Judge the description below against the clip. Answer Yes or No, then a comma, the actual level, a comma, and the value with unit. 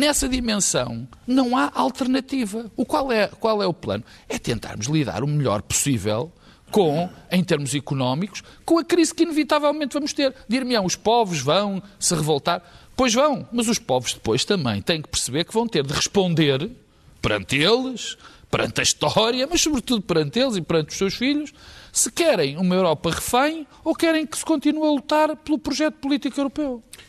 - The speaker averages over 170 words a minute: Yes, average, 180 wpm